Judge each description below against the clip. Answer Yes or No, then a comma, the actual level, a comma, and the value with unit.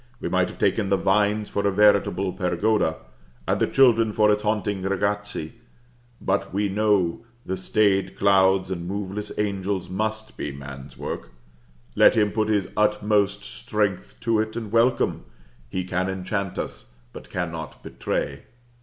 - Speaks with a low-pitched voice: Yes, low, 100 Hz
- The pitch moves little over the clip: Yes, narrow, 2.2 semitones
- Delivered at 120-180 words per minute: Yes, average, 150 wpm